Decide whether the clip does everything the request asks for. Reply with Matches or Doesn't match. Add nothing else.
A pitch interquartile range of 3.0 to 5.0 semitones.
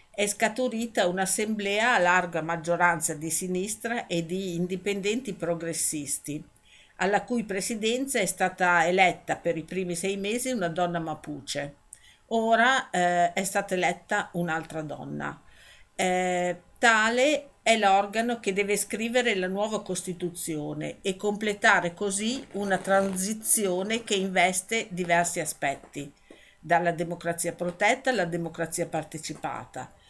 Matches